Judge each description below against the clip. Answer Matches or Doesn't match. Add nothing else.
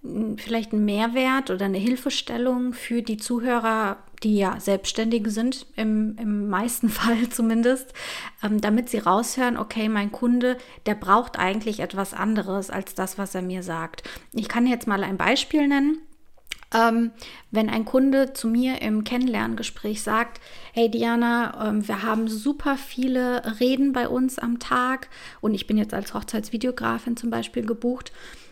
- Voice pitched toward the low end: Doesn't match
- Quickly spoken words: Doesn't match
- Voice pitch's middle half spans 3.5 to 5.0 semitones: Doesn't match